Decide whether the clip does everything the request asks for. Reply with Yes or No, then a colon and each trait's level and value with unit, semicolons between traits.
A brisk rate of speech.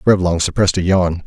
No: average, 190 wpm